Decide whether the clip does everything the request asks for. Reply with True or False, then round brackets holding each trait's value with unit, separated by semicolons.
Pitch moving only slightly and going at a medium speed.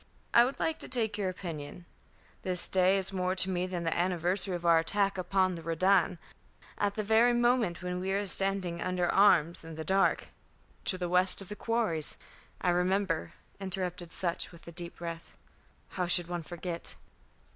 True (2.2 semitones; 185 wpm)